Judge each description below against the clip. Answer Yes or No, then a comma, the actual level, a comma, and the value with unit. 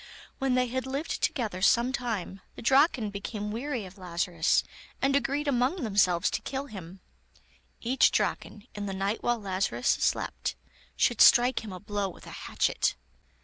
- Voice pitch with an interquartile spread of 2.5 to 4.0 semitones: No, average, 5.1 semitones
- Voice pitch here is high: Yes, high, 220 Hz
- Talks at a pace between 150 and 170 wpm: Yes, average, 160 wpm